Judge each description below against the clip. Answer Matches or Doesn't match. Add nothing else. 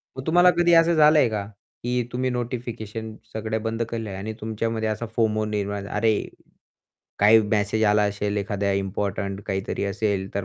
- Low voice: Matches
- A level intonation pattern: Matches